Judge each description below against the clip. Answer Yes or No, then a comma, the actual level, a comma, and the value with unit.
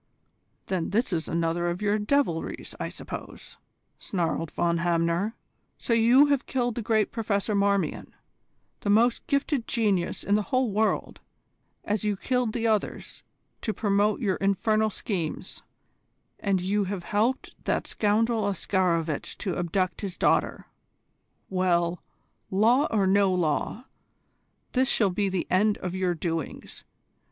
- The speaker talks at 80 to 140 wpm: Yes, slow, 135 wpm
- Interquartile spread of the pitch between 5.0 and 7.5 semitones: No, average, 3.7 semitones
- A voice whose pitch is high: Yes, high, 200 Hz